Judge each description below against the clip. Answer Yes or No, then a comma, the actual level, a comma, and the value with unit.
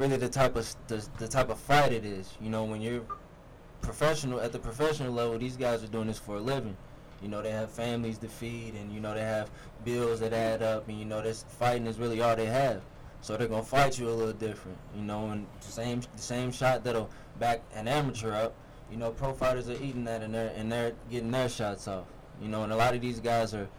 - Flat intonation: Yes, narrow, 2.2 semitones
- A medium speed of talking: No, fast, 245 wpm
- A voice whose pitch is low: Yes, low, 115 Hz